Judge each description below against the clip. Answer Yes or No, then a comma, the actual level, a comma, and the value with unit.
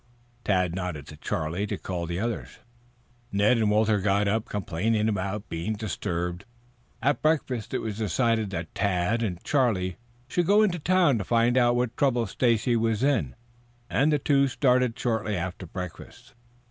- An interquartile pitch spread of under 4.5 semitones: No, average, 4.9 semitones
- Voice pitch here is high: No, low, 110 Hz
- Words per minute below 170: Yes, average, 160 wpm